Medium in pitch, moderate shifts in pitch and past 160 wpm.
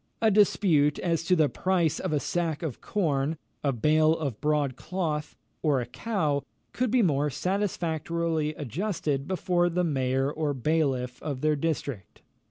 No: medium, 155 Hz; average, 3.6 semitones; average, 155 wpm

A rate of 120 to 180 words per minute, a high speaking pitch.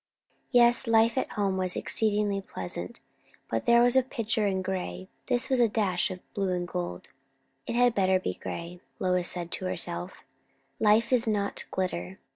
Yes: average, 170 wpm; high, 195 Hz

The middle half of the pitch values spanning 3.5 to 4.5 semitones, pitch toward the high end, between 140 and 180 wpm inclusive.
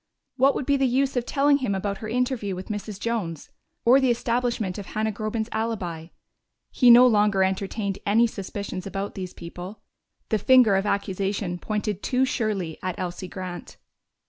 Yes: average, 3.8 semitones; high, 210 Hz; average, 170 wpm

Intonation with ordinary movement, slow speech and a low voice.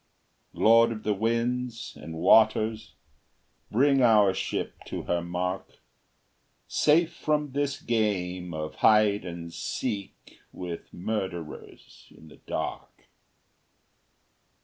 Yes: average, 4.7 semitones; slow, 105 wpm; low, 105 Hz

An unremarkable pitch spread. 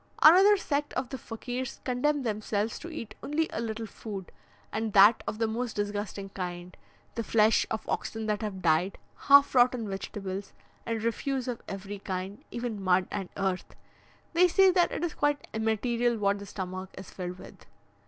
Yes: average, 4.3 semitones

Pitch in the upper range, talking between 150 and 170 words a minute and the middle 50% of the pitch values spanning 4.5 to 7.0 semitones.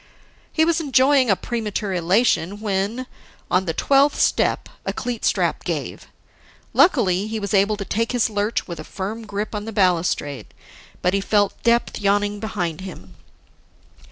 No: high, 205 Hz; average, 155 wpm; average, 3.5 semitones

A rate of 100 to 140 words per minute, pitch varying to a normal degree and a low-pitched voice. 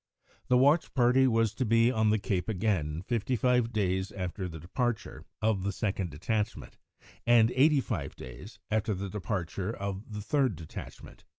No: average, 165 wpm; average, 4.2 semitones; low, 105 Hz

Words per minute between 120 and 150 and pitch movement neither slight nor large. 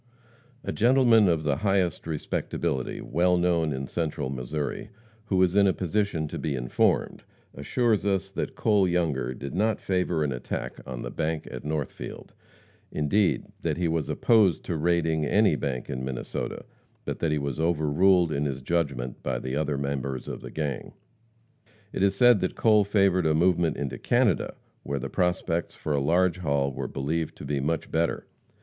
No: average, 175 wpm; average, 4.8 semitones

